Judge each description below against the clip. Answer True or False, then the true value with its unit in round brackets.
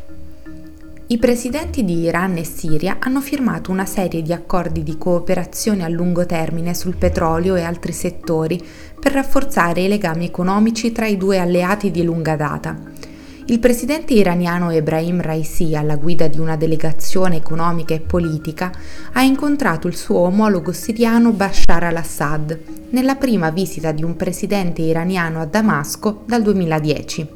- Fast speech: False (145 wpm)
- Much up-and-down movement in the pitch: False (4.4 semitones)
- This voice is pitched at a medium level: True (175 Hz)